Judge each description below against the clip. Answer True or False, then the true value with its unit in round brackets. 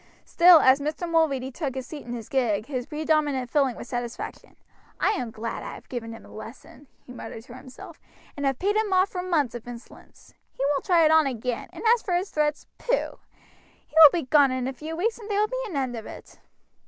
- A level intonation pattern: False (5.2 semitones)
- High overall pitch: True (280 Hz)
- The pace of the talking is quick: True (230 wpm)